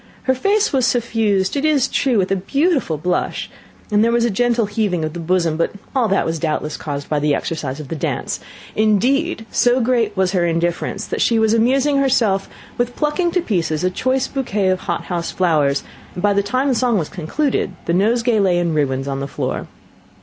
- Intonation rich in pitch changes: Yes, wide, 6.6 semitones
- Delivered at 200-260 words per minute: Yes, fast, 205 wpm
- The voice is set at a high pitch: Yes, high, 205 Hz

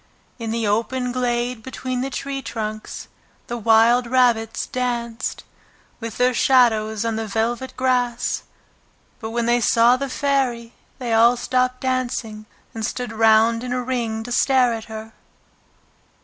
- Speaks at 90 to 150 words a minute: Yes, average, 145 wpm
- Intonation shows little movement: Yes, narrow, 2.1 semitones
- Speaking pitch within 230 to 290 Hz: Yes, high, 240 Hz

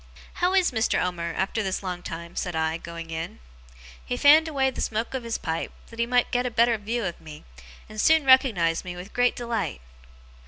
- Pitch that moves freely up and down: Yes, wide, 6.5 semitones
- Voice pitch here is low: No, high, 215 Hz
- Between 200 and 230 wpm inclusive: Yes, fast, 205 wpm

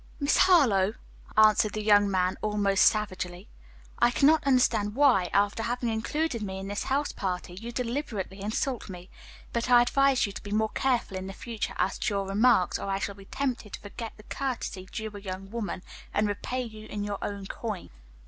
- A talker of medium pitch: No, high, 210 Hz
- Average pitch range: Yes, average, 3.6 semitones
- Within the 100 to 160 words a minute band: No, average, 195 wpm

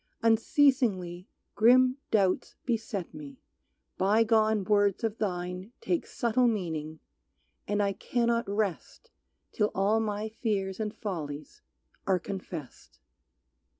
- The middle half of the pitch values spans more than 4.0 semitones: No, average, 3.4 semitones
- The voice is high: Yes, high, 210 Hz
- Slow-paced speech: Yes, slow, 105 wpm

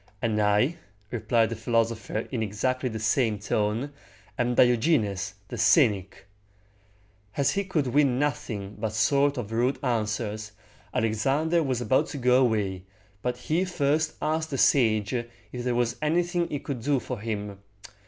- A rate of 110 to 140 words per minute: No, average, 150 wpm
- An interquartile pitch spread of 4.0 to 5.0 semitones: Yes, average, 4.5 semitones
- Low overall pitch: Yes, low, 120 Hz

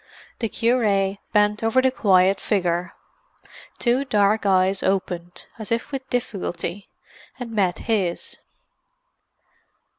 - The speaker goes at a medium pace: No, slow, 110 wpm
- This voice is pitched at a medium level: No, high, 205 Hz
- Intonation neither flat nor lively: Yes, average, 3.5 semitones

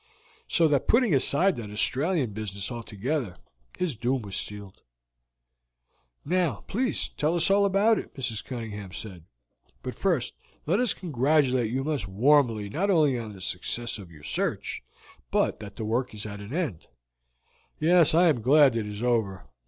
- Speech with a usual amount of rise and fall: No, wide, 7.2 semitones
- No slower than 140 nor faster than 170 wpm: Yes, average, 160 wpm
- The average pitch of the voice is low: Yes, low, 125 Hz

